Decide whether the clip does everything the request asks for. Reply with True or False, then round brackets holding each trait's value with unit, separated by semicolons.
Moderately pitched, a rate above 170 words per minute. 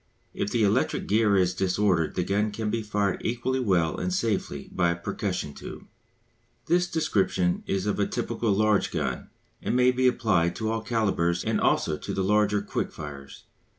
False (105 Hz; 180 wpm)